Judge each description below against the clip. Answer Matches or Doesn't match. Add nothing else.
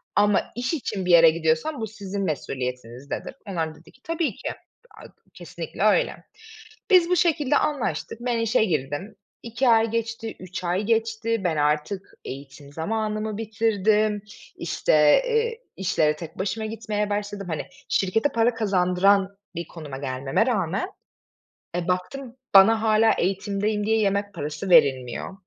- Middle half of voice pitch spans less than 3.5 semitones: Doesn't match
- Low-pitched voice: Doesn't match